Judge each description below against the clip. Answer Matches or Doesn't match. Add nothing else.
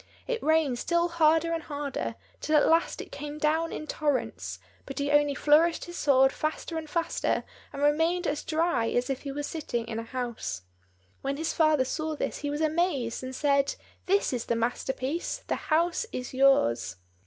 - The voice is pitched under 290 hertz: Doesn't match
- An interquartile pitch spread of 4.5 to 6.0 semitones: Doesn't match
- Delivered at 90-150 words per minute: Doesn't match